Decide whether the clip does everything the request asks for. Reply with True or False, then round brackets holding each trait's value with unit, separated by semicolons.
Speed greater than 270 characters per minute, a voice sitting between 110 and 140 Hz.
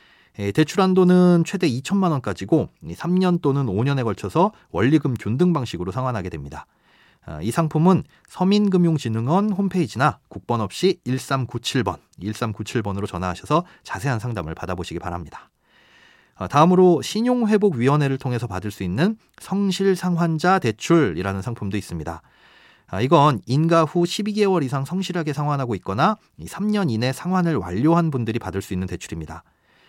True (325 characters per minute; 135 Hz)